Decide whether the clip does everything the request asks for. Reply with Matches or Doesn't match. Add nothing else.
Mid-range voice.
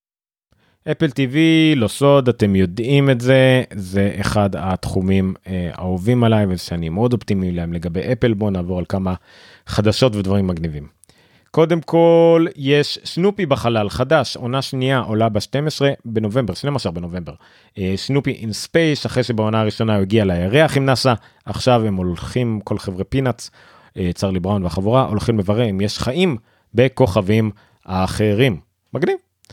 Doesn't match